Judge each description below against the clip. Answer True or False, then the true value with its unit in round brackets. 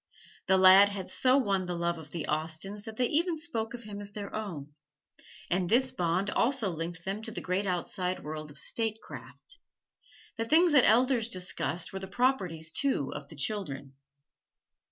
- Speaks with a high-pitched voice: True (195 Hz)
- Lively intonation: False (5.0 semitones)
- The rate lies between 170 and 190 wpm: True (175 wpm)